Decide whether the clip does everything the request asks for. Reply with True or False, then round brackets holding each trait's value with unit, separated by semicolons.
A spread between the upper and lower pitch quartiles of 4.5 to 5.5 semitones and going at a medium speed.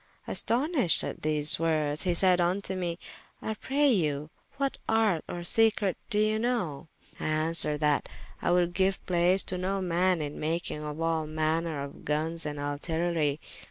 False (3.7 semitones; 160 wpm)